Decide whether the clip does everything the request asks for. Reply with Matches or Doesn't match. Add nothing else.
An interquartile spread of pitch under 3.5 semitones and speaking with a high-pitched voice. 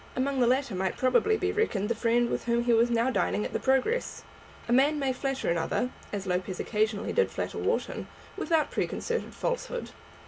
Doesn't match